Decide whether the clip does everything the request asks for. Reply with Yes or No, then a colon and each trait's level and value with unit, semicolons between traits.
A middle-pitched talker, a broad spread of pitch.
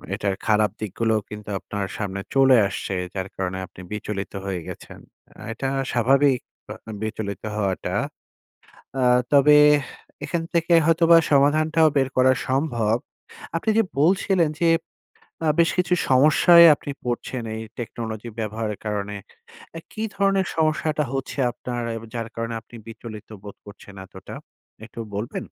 No: low, 120 Hz; wide, 6.5 semitones